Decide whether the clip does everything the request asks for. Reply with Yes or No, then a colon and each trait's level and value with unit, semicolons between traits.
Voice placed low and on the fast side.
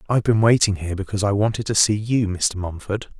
Yes: low, 105 Hz; fast, 225 wpm